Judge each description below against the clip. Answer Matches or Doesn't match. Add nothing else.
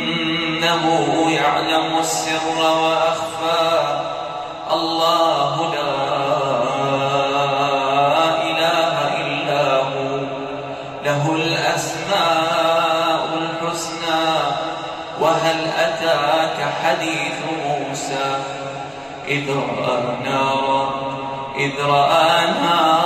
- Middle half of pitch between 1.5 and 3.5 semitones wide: Matches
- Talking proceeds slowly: Matches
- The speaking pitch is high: Doesn't match